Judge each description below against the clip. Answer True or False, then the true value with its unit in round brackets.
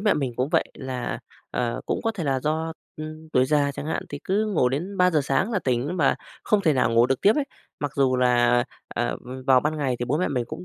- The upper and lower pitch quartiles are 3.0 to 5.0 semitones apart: True (4.2 semitones)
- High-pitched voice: False (145 Hz)